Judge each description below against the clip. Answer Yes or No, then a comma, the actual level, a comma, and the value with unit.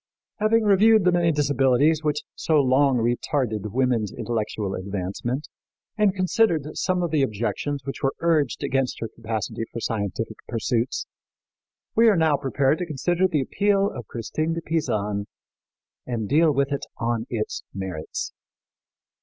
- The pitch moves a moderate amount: No, wide, 6.4 semitones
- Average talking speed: Yes, average, 145 wpm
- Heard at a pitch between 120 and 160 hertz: Yes, low, 135 Hz